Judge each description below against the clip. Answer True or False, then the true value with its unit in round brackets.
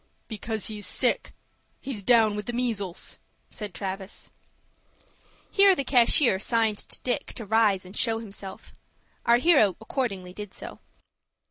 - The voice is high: True (220 Hz)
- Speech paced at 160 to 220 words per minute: False (135 wpm)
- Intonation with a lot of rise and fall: False (3.4 semitones)